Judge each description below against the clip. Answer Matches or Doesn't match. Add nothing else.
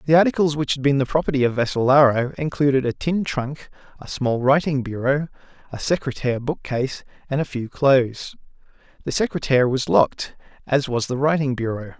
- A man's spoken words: Matches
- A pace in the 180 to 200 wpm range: Doesn't match